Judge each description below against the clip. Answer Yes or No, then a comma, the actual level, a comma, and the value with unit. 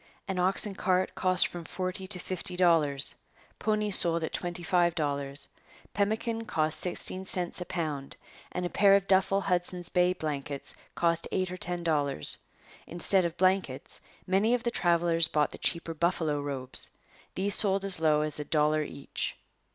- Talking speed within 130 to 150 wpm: No, average, 165 wpm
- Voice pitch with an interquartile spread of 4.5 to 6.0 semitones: No, average, 3.4 semitones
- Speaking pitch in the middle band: Yes, medium, 175 Hz